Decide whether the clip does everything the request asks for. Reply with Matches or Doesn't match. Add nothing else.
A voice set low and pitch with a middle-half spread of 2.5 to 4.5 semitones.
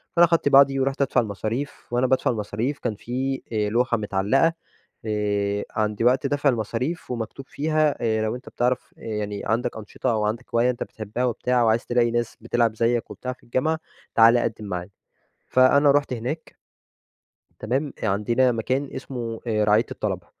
Matches